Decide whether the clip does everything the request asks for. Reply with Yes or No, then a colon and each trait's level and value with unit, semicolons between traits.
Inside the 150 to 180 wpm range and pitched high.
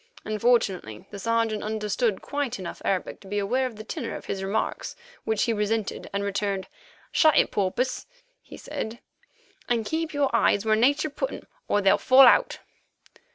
Yes: average, 170 wpm; high, 220 Hz